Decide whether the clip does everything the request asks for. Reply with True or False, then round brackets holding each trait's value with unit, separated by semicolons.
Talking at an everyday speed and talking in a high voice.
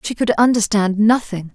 True (155 wpm; 215 Hz)